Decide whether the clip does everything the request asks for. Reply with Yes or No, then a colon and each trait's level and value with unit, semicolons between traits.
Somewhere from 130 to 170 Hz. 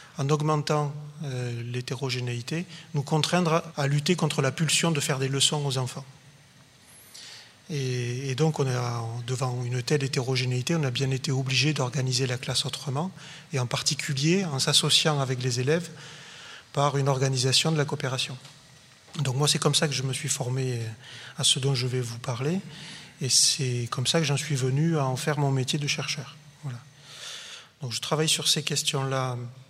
Yes: medium, 140 Hz